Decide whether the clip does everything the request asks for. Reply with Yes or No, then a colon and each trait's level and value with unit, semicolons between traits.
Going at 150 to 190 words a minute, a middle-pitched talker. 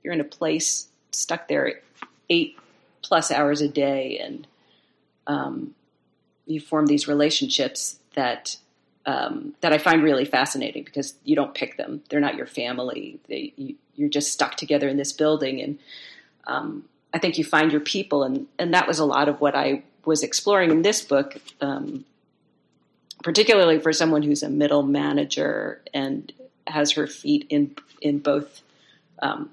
Yes: average, 165 wpm; medium, 155 Hz